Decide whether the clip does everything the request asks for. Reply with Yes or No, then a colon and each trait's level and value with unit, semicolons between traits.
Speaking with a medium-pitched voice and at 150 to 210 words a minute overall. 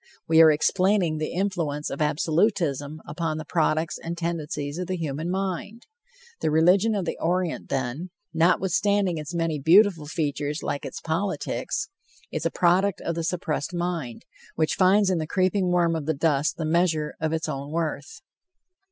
Yes: medium, 165 Hz; average, 165 wpm